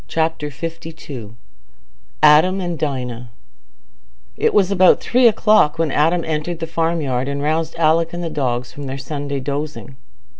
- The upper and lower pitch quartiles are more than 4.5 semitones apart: No, average, 2.9 semitones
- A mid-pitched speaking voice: Yes, medium, 155 Hz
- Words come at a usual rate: Yes, average, 145 wpm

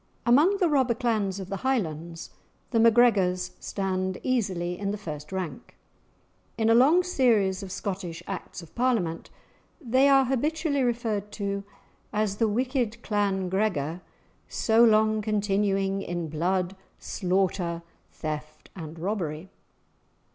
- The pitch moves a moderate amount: Yes, average, 4.5 semitones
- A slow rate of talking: Yes, slow, 125 wpm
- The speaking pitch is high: Yes, high, 200 Hz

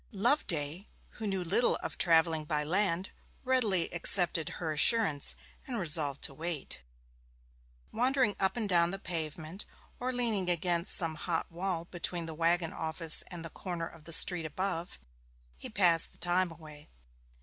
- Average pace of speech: Yes, average, 150 wpm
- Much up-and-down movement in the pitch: No, average, 3.1 semitones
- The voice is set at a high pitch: No, medium, 175 Hz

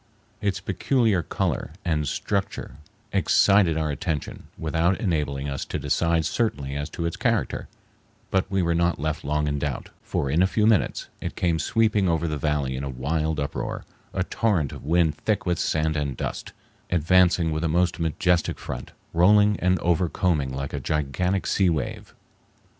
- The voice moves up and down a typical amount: Yes, average, 3.8 semitones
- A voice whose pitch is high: No, very low, 85 Hz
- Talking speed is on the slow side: No, average, 170 wpm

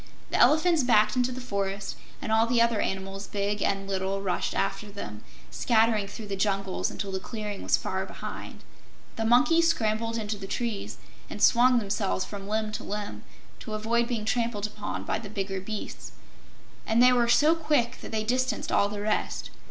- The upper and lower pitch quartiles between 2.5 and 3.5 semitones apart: Yes, average, 3.0 semitones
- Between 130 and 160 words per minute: No, average, 185 wpm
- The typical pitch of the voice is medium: No, high, 215 Hz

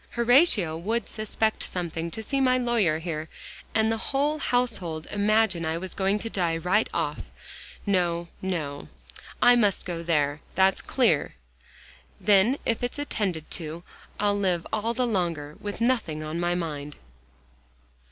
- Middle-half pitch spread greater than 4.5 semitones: Yes, average, 5.2 semitones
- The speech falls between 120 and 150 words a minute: Yes, average, 145 wpm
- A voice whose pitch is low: No, high, 190 Hz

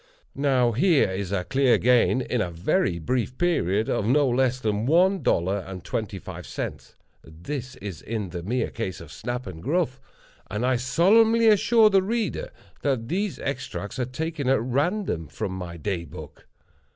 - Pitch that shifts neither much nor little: No, wide, 7.6 semitones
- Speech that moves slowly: No, average, 165 wpm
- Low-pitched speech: Yes, low, 125 Hz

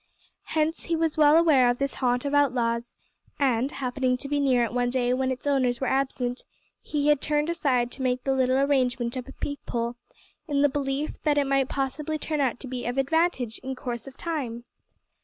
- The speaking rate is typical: No, fast, 210 wpm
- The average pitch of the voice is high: Yes, very high, 265 Hz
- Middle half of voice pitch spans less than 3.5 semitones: Yes, average, 2.7 semitones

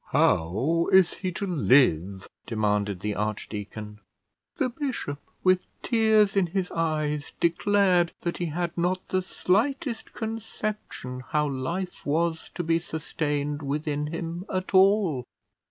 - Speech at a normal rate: No, slow, 125 wpm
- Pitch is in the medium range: Yes, medium, 165 Hz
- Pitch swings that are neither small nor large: Yes, average, 4.9 semitones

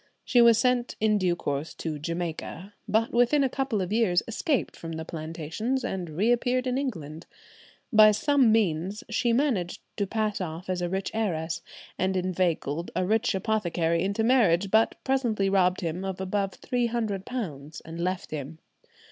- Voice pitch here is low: No, high, 195 Hz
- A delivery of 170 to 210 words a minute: No, average, 160 wpm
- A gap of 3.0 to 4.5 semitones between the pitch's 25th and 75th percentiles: No, average, 5.3 semitones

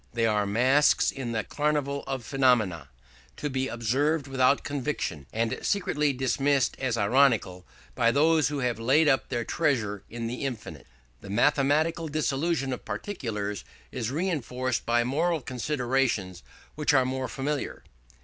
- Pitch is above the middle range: No, low, 130 Hz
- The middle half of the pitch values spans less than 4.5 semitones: Yes, average, 3.9 semitones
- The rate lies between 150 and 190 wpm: No, average, 140 wpm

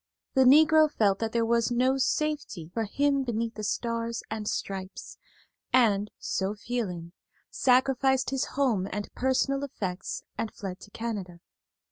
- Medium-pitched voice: No, high, 230 Hz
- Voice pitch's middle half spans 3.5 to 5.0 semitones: Yes, average, 4.4 semitones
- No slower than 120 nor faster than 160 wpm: Yes, average, 140 wpm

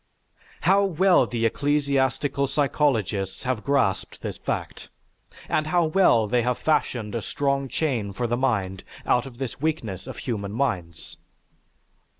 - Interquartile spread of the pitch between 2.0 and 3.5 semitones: No, average, 4.8 semitones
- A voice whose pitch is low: Yes, low, 130 Hz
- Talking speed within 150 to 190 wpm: No, average, 140 wpm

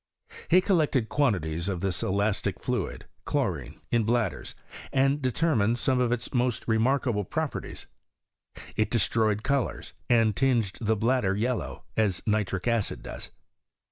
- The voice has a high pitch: No, low, 115 Hz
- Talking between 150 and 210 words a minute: No, average, 140 wpm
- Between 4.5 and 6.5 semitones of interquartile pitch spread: No, average, 3.9 semitones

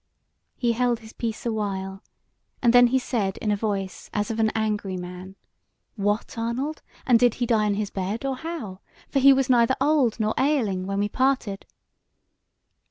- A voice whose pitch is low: No, high, 225 Hz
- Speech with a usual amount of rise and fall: Yes, average, 3.7 semitones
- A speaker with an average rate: Yes, average, 175 wpm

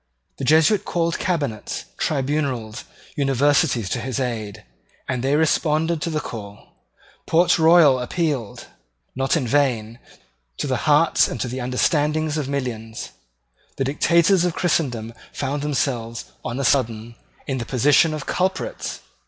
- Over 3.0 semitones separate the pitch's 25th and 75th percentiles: Yes, average, 4.4 semitones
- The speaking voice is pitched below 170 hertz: Yes, medium, 140 Hz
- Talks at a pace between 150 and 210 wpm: No, slow, 135 wpm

